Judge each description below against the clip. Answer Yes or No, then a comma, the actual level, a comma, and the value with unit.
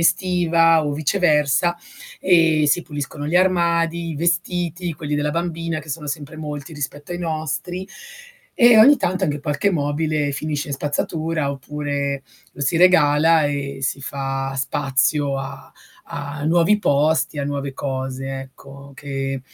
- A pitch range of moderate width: Yes, average, 3.0 semitones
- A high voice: No, medium, 150 Hz